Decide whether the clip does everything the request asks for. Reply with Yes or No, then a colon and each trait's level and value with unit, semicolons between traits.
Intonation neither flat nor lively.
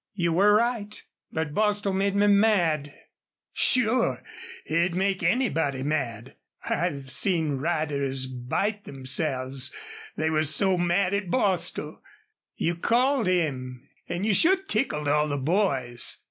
No: wide, 6.1 semitones